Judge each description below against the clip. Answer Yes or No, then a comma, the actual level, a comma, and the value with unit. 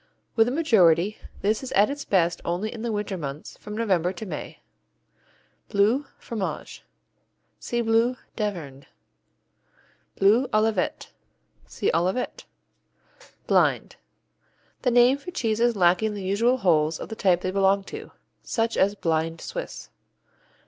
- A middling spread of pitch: Yes, average, 4.5 semitones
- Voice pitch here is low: No, high, 205 Hz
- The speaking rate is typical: No, slow, 130 wpm